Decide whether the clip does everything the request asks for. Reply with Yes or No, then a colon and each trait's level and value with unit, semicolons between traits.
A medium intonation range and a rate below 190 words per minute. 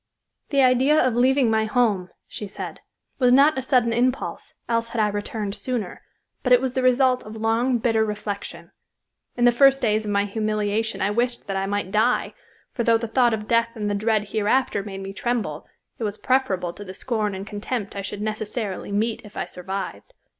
No: average, 3.2 semitones; average, 200 wpm